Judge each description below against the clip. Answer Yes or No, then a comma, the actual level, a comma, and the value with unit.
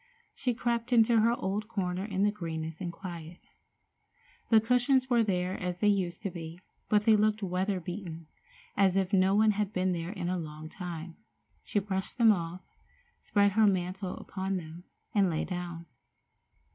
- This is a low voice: No, high, 190 Hz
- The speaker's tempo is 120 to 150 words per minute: No, average, 170 wpm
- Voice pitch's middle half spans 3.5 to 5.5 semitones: No, average, 3.1 semitones